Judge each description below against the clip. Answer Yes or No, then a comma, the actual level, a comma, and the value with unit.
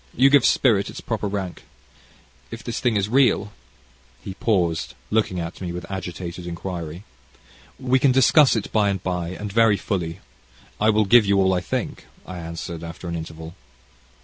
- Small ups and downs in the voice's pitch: No, average, 4.3 semitones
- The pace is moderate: Yes, average, 175 wpm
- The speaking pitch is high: No, very low, 95 Hz